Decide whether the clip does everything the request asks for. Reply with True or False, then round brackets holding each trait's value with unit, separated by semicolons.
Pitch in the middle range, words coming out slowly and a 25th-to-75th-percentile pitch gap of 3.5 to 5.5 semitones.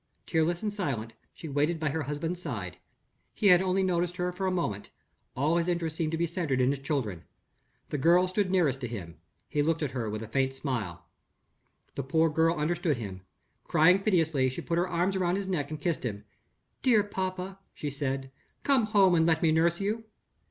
False (160 Hz; 200 wpm; 4.9 semitones)